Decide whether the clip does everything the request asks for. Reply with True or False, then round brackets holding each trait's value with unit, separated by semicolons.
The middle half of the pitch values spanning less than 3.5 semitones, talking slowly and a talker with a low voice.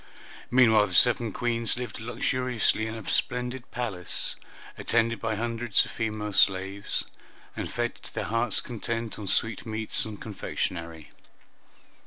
True (2.4 semitones; 130 wpm; 115 Hz)